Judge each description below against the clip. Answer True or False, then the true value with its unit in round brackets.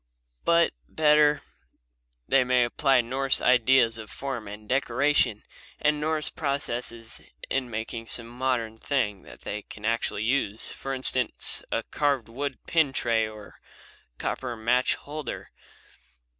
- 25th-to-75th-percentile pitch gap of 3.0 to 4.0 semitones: True (3.4 semitones)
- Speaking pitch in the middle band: False (125 Hz)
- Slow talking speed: True (130 wpm)